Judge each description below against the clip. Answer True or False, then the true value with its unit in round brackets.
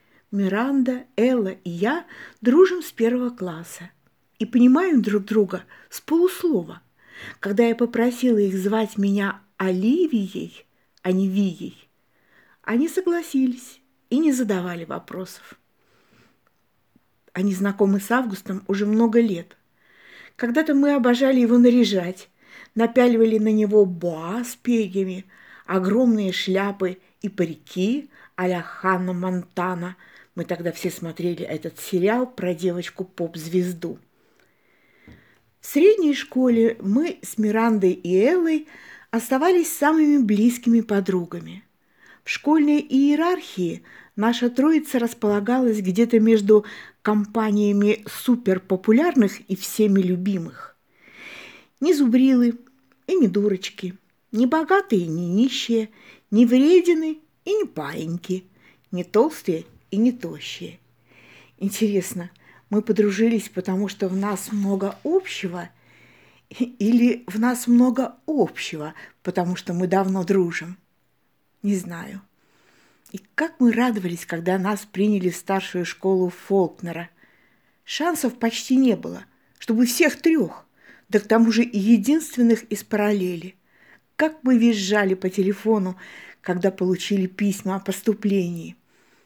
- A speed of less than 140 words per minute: True (110 wpm)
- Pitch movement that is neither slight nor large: True (4.7 semitones)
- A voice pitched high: True (210 Hz)